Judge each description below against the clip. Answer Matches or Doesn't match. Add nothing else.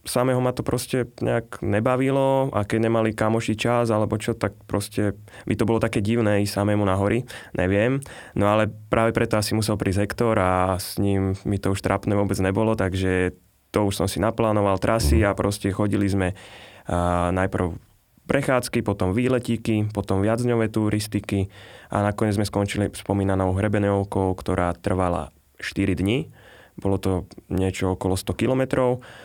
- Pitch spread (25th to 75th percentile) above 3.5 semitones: Doesn't match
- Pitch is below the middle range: Matches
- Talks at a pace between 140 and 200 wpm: Matches